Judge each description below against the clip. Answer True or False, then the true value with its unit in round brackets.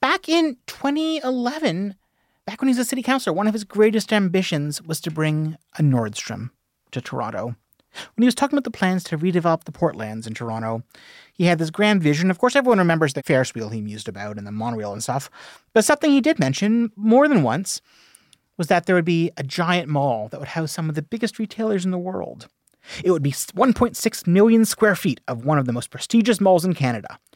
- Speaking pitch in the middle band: True (180 Hz)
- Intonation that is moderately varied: False (7.9 semitones)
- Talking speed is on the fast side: True (215 wpm)